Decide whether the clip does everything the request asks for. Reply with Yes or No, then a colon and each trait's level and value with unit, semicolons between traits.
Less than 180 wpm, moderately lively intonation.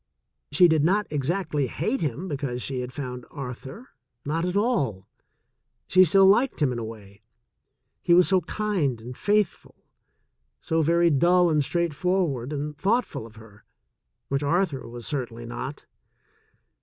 No: average, 155 wpm; wide, 6.2 semitones